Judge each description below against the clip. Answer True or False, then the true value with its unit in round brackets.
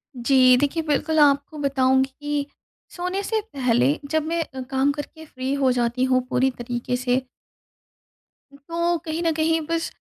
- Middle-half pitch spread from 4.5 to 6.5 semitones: False (3.8 semitones)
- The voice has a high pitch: True (280 Hz)